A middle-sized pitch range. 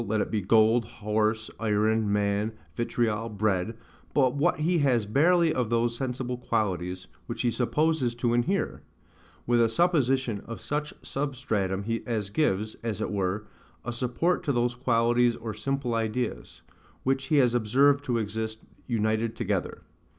Yes: average, 3.4 semitones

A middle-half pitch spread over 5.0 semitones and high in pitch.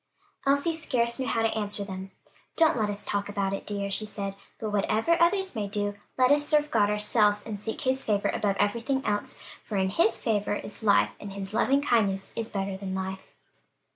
No: average, 3.0 semitones; high, 210 Hz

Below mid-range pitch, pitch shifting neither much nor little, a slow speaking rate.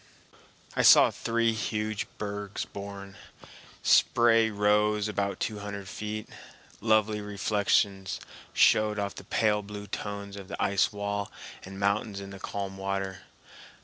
No: low, 100 Hz; narrow, 1.3 semitones; slow, 130 wpm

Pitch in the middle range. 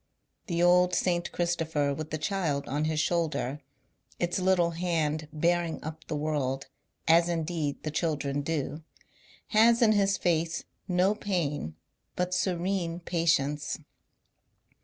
Yes: medium, 165 Hz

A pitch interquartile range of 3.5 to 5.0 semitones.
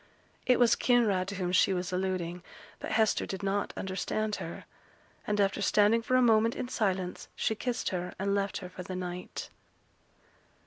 No: average, 3.1 semitones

